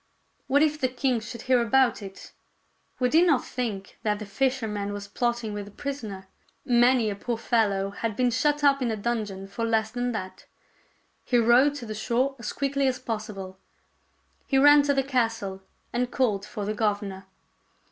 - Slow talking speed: No, average, 180 wpm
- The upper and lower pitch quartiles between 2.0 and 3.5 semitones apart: No, average, 3.9 semitones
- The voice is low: No, high, 235 Hz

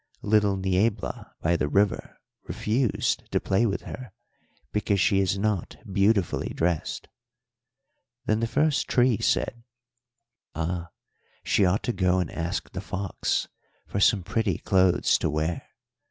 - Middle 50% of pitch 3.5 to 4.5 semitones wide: No, average, 3.0 semitones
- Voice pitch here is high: No, low, 100 Hz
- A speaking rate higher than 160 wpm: No, slow, 135 wpm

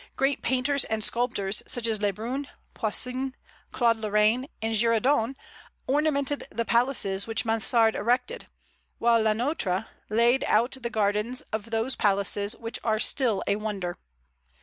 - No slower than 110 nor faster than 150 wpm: Yes, average, 140 wpm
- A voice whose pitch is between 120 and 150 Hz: No, high, 230 Hz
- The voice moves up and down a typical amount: Yes, average, 3.0 semitones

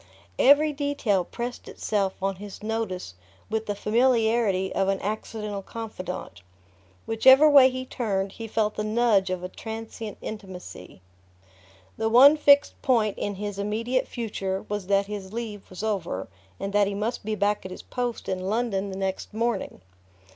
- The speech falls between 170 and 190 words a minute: No, average, 160 wpm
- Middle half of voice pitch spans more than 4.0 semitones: No, average, 3.2 semitones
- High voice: Yes, high, 210 Hz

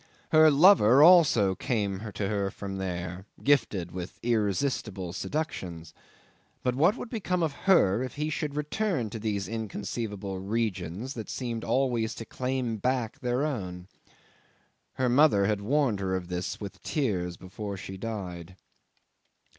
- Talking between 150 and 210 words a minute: No, average, 140 wpm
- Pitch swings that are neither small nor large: No, wide, 5.8 semitones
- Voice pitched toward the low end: Yes, low, 110 Hz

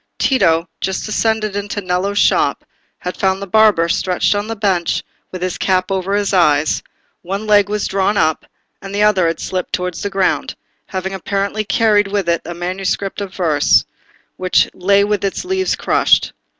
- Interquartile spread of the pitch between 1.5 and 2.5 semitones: Yes, narrow, 2.1 semitones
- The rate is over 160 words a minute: Yes, average, 175 wpm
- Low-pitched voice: No, high, 195 Hz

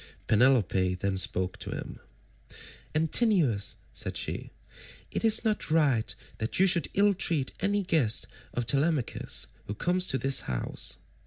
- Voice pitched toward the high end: No, medium, 140 Hz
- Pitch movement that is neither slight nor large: No, wide, 8.8 semitones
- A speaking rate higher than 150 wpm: No, average, 140 wpm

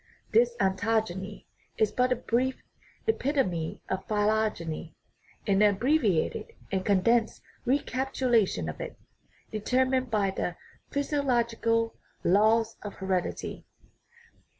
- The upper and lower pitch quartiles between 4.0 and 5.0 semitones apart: Yes, average, 4.5 semitones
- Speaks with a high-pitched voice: Yes, high, 220 Hz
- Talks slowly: Yes, slow, 100 wpm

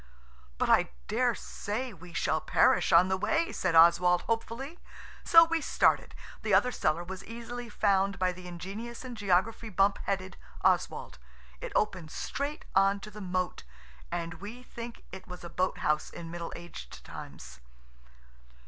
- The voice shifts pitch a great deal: No, average, 4.6 semitones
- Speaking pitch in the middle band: No, high, 195 Hz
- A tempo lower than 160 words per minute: Yes, average, 150 wpm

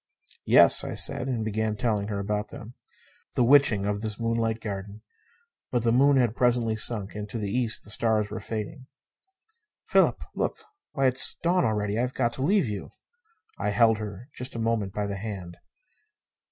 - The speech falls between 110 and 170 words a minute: No, average, 180 wpm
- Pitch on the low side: Yes, low, 110 Hz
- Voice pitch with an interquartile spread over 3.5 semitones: No, average, 2.8 semitones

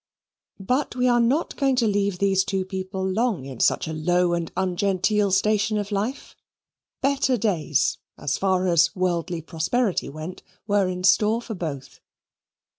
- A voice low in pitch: No, high, 190 Hz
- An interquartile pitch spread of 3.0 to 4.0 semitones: Yes, average, 3.5 semitones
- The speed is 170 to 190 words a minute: No, average, 155 wpm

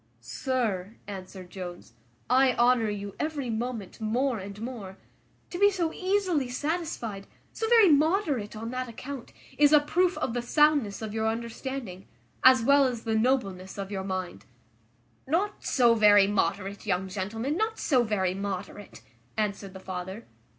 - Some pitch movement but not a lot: No, wide, 5.9 semitones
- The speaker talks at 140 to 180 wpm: Yes, average, 150 wpm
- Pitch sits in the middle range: No, high, 230 Hz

